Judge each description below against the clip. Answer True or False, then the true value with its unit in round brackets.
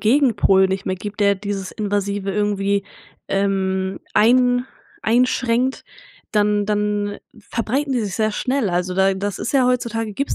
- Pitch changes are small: False (3.1 semitones)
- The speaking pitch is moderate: False (205 Hz)